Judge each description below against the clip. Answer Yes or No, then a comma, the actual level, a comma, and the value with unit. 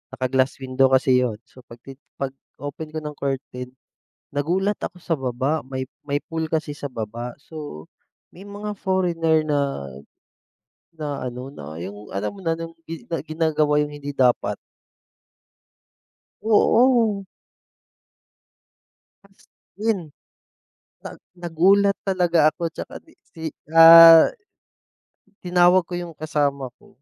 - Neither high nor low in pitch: Yes, medium, 155 Hz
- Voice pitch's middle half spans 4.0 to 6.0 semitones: Yes, average, 4.6 semitones